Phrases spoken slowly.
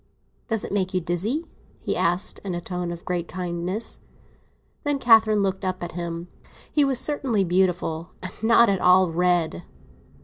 No: average, 165 wpm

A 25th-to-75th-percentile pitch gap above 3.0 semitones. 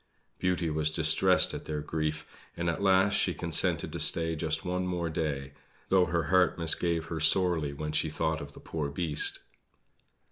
No: narrow, 2.6 semitones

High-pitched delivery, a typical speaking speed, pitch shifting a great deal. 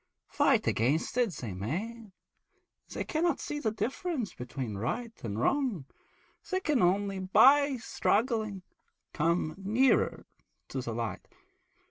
No: high, 215 Hz; slow, 125 wpm; wide, 8.6 semitones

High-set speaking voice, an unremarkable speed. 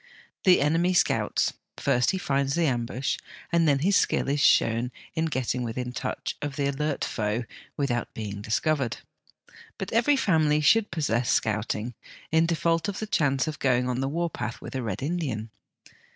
No: medium, 140 Hz; average, 170 wpm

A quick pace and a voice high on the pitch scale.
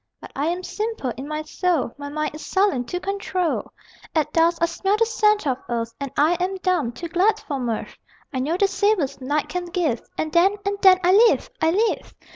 Yes: fast, 215 wpm; very high, 340 Hz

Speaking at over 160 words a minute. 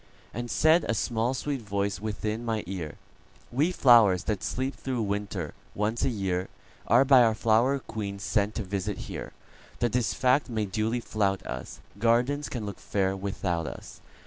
No: average, 150 wpm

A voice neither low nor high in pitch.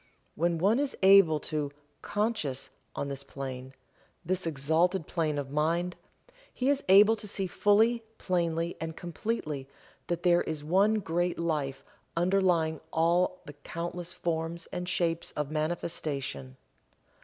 Yes: medium, 170 Hz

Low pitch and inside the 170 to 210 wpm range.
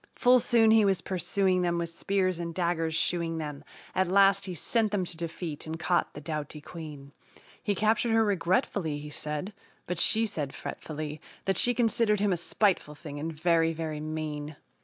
No: medium, 170 Hz; average, 180 wpm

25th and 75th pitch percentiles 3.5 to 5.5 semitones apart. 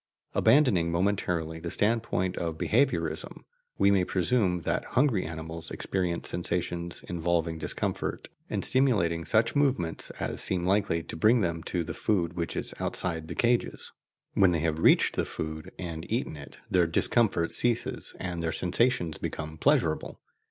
Yes: average, 4.2 semitones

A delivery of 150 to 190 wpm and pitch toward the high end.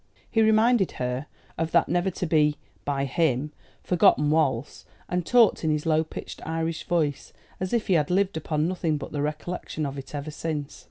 No: average, 185 wpm; medium, 160 Hz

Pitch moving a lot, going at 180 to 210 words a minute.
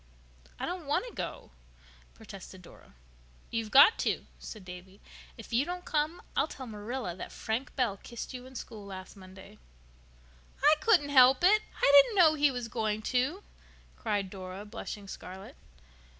No: wide, 6.2 semitones; average, 160 wpm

